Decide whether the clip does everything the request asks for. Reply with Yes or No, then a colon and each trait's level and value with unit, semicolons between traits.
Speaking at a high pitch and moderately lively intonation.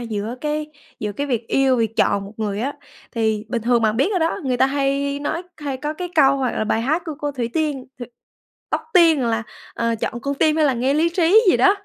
Yes: very high, 270 Hz; average, 4.8 semitones